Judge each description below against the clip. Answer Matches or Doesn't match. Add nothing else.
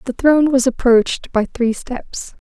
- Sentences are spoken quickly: Doesn't match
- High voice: Matches